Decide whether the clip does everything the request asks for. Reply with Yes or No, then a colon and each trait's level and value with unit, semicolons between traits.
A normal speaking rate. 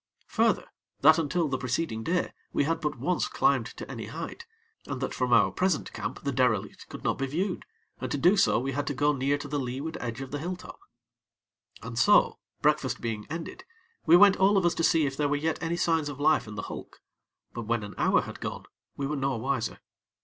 No: fast, 225 wpm